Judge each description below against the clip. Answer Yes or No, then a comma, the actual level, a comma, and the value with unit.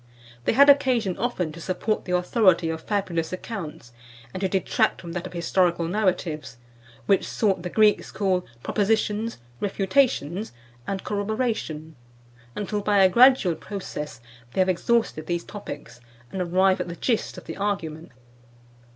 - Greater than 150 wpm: No, average, 145 wpm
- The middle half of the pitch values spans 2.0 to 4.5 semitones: Yes, average, 3.7 semitones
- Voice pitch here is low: No, high, 190 Hz